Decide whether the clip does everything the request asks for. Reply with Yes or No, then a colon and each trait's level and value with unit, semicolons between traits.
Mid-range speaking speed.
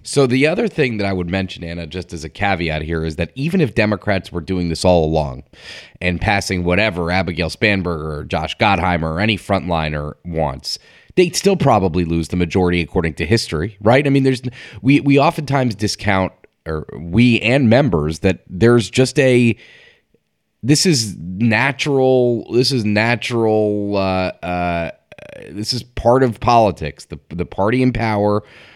Yes: average, 165 wpm